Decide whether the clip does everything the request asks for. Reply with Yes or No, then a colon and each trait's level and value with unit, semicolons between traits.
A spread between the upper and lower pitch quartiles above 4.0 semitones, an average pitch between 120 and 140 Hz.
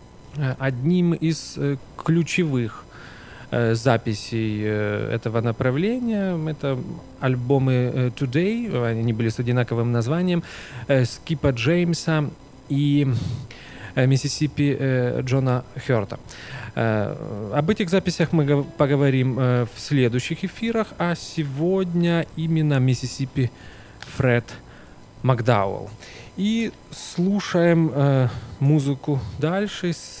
Yes: average, 4.8 semitones; low, 135 Hz